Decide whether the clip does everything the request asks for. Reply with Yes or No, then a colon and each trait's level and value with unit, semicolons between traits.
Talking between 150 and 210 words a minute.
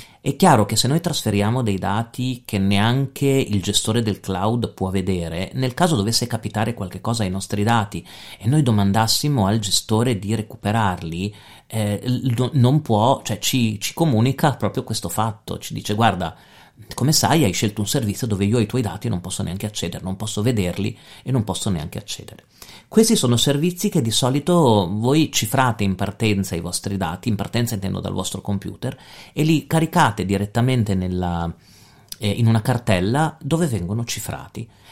Yes: fast, 170 wpm